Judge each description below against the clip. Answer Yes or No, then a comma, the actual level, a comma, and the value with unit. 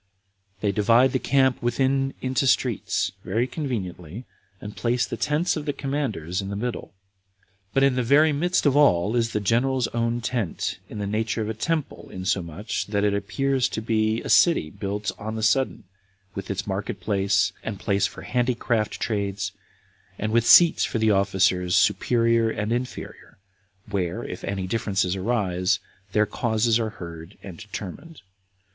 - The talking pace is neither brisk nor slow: Yes, average, 165 wpm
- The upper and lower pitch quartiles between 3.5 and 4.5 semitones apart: Yes, average, 4.1 semitones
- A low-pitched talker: Yes, low, 110 Hz